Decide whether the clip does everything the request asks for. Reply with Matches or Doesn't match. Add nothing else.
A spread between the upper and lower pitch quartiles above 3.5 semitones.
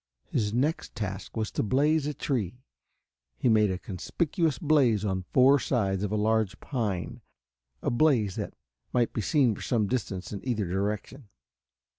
Matches